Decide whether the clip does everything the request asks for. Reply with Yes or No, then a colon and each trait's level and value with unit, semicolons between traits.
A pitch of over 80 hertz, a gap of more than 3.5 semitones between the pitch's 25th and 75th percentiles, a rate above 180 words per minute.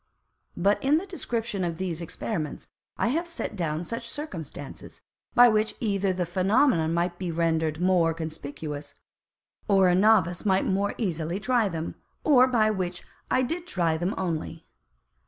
No: medium, 185 Hz; average, 5.1 semitones; average, 155 wpm